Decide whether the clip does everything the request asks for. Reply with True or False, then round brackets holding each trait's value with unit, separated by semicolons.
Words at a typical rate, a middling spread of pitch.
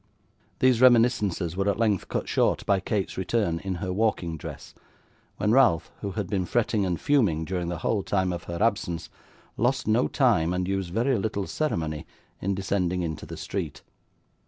True (175 wpm; 4.3 semitones)